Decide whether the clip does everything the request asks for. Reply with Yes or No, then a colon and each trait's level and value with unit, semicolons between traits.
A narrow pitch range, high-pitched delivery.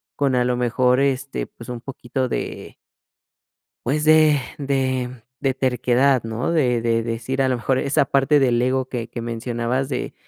No: narrow, 2.1 semitones; low, 130 Hz